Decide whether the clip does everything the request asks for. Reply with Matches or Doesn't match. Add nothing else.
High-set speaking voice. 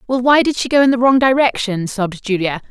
Matches